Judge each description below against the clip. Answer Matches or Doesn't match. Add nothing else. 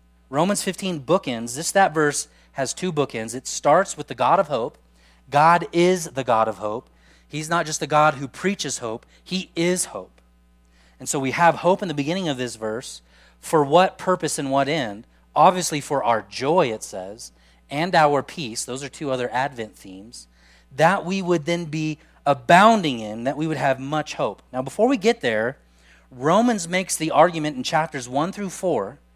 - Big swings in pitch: Matches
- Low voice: Doesn't match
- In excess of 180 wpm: Matches